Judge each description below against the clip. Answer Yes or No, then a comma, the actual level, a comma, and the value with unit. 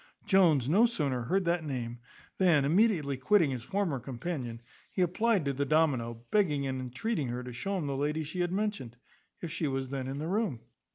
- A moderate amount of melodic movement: No, wide, 5.9 semitones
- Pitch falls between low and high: Yes, medium, 150 Hz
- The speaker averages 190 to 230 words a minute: Yes, average, 195 wpm